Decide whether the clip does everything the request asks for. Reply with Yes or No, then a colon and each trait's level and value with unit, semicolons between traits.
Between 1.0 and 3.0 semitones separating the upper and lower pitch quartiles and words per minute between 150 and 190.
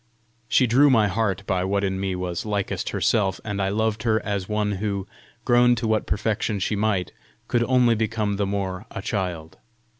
Yes: narrow, 2.5 semitones; average, 185 wpm